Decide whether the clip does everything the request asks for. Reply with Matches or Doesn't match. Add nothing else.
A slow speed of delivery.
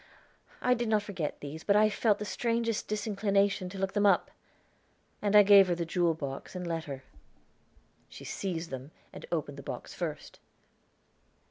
Doesn't match